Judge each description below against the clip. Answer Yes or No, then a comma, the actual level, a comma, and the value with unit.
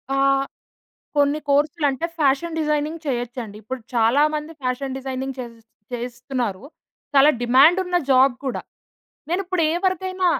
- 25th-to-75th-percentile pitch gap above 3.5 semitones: Yes, average, 3.9 semitones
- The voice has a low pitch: No, very high, 275 Hz